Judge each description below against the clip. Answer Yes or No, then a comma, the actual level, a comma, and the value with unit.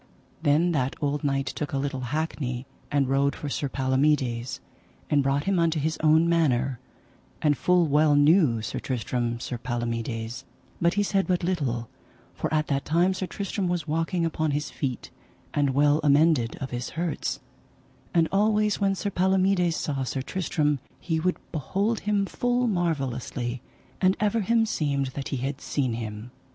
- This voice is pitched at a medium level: Yes, medium, 150 Hz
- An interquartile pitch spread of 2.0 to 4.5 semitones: No, average, 4.9 semitones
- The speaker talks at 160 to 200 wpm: Yes, average, 165 wpm